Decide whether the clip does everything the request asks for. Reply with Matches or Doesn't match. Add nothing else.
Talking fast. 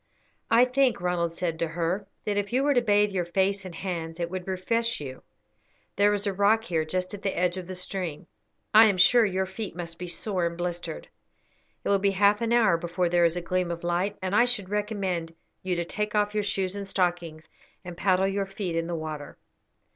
Matches